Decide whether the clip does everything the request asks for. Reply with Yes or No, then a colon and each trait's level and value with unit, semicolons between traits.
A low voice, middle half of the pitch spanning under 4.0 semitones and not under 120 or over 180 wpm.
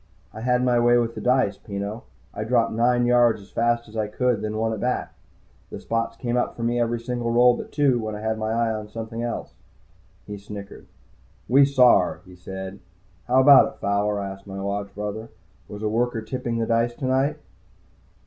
No: low, 115 Hz; narrow, 2.6 semitones; fast, 205 wpm